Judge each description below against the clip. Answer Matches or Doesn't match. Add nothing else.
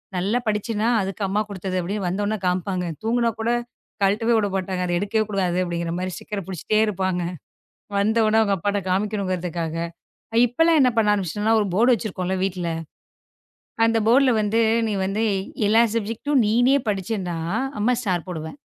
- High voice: Matches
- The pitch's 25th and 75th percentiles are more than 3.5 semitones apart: Doesn't match